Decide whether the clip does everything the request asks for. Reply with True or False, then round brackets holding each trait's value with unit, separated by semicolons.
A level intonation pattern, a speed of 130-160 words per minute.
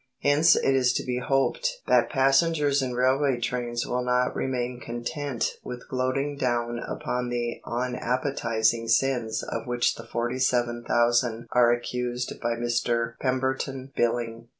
True (1.9 semitones; 140 wpm)